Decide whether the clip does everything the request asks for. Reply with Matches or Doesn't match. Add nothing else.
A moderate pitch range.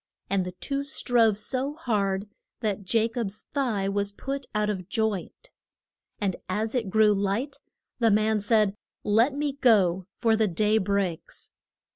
Matches